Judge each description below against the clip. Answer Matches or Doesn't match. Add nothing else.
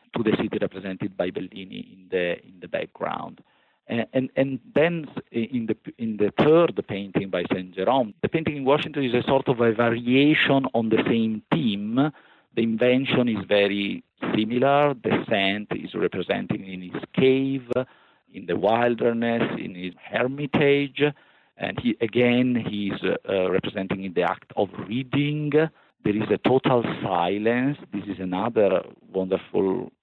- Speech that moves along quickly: Doesn't match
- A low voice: Matches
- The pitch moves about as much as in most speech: Matches